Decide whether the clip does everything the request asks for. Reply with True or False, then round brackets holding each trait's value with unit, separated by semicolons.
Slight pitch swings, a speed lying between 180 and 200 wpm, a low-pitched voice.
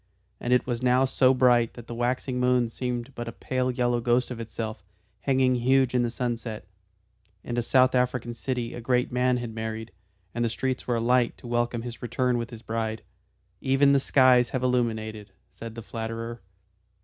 True (1.6 semitones; 185 wpm; 120 Hz)